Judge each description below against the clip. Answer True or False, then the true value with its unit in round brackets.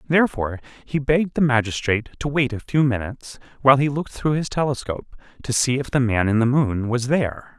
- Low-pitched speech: True (130 Hz)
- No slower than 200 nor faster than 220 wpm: True (205 wpm)